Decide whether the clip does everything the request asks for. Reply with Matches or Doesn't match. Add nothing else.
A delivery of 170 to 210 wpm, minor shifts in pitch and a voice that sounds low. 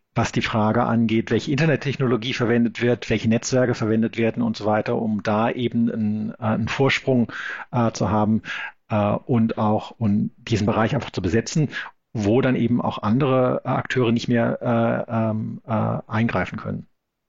Doesn't match